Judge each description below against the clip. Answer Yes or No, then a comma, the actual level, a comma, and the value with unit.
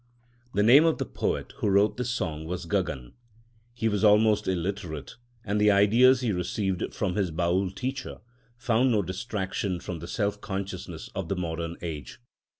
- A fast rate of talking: No, average, 165 wpm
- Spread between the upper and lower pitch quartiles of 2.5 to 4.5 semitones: Yes, average, 3.5 semitones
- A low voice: Yes, low, 100 Hz